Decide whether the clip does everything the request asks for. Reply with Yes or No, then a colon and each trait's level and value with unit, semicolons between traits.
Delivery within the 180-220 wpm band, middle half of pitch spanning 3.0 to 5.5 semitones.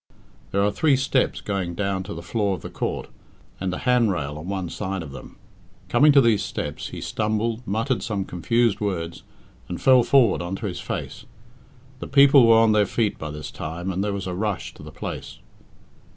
Yes: average, 200 wpm; average, 4.3 semitones